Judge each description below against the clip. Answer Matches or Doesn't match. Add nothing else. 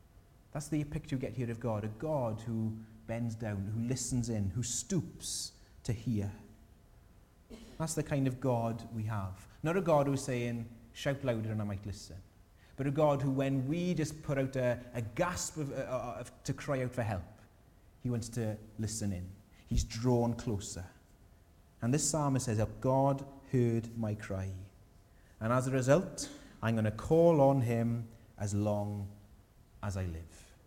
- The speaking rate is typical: Matches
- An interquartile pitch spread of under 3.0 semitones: Doesn't match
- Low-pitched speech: Matches